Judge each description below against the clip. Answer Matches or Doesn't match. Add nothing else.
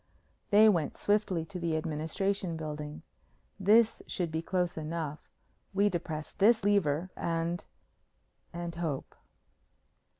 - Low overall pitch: Doesn't match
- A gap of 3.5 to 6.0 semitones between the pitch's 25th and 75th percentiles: Matches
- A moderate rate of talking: Doesn't match